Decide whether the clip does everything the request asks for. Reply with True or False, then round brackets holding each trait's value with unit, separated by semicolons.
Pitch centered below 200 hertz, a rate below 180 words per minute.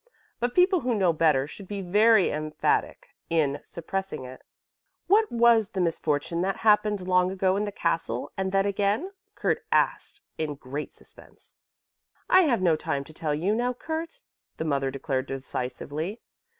True (185 Hz; 160 wpm)